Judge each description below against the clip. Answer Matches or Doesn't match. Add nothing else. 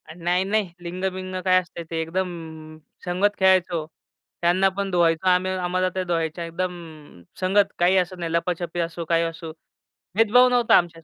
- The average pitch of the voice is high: Doesn't match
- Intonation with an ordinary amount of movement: Doesn't match